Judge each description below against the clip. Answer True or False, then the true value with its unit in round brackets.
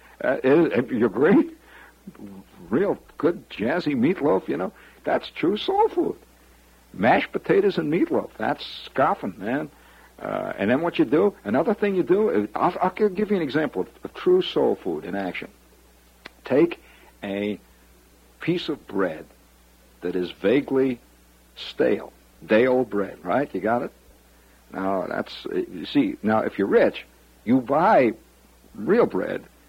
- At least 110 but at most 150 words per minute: True (140 wpm)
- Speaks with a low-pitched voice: True (110 Hz)